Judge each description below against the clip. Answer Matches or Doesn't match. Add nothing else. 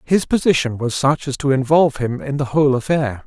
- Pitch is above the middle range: Doesn't match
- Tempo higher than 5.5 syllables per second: Matches